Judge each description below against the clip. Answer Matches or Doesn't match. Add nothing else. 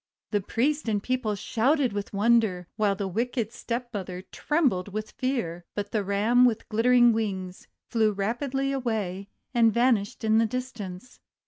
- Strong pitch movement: Doesn't match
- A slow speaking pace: Doesn't match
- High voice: Matches